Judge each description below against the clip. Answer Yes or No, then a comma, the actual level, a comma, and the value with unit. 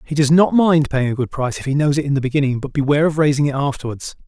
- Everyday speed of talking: No, fast, 295 wpm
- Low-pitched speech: No, medium, 145 Hz